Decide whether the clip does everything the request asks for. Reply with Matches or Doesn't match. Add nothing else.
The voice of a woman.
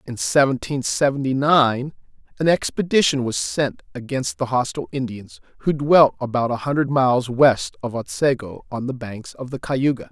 Doesn't match